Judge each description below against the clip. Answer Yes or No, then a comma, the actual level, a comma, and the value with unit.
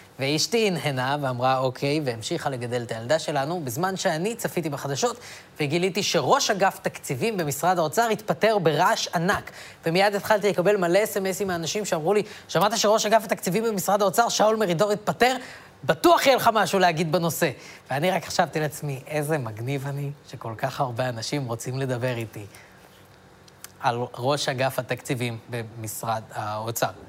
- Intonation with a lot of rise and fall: Yes, wide, 7.4 semitones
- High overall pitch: No, medium, 160 Hz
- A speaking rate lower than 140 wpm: No, average, 145 wpm